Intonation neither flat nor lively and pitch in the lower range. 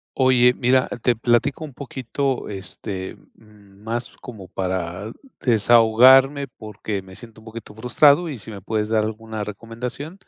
Yes: average, 3.3 semitones; low, 115 Hz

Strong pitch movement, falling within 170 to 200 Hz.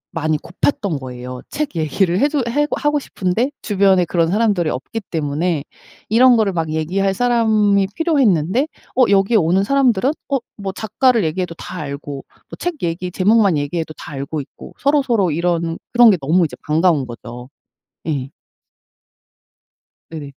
Yes: wide, 6.4 semitones; medium, 185 Hz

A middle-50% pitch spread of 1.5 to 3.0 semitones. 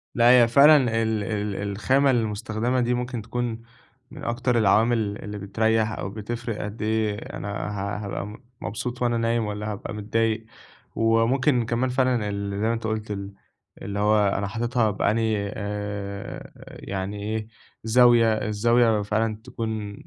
Yes: narrow, 2.4 semitones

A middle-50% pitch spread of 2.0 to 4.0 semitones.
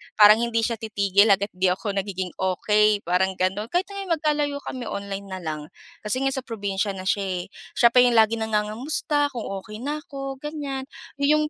No: wide, 5.4 semitones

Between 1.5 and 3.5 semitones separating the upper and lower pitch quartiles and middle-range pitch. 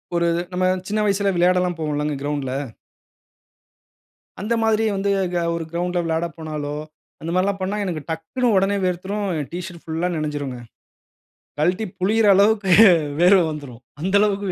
No: average, 4.0 semitones; medium, 180 Hz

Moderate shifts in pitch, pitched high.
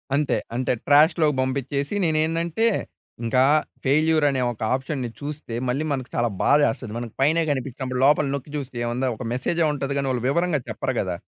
No: average, 3.0 semitones; medium, 140 Hz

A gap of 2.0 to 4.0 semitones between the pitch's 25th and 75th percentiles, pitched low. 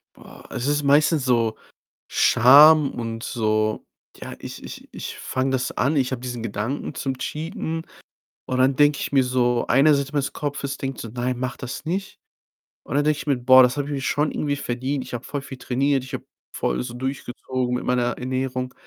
Yes: narrow, 2.5 semitones; low, 130 Hz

